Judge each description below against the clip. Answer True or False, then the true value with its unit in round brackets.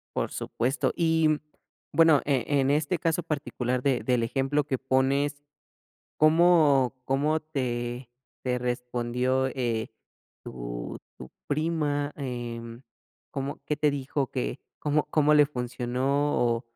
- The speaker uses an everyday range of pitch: True (3.2 semitones)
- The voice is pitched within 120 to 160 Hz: True (135 Hz)